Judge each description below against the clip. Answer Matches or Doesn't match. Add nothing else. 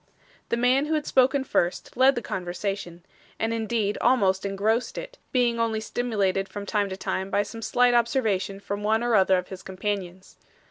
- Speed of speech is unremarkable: Matches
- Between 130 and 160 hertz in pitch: Doesn't match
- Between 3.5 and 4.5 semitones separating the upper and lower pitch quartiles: Matches